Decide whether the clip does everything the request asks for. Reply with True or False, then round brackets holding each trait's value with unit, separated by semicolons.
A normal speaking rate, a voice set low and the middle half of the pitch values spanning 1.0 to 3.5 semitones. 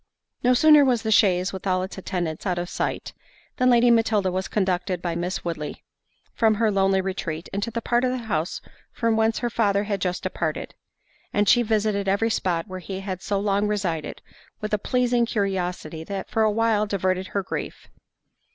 False (190 wpm; 200 Hz; 3.2 semitones)